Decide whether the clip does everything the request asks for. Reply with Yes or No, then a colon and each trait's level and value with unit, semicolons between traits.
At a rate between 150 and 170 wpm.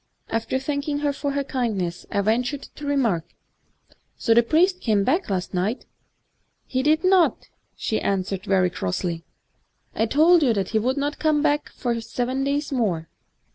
No: average, 185 wpm